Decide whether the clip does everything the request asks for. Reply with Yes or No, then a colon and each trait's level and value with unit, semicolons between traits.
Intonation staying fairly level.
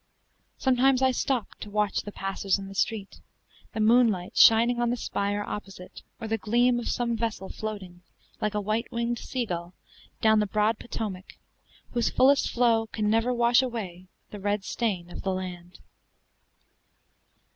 No: average, 3.3 semitones